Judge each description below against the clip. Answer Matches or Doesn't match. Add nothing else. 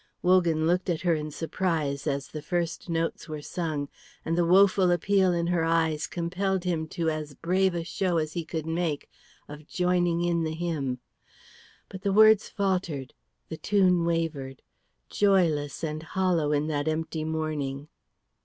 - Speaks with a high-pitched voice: Doesn't match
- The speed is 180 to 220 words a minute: Doesn't match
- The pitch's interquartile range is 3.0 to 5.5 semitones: Doesn't match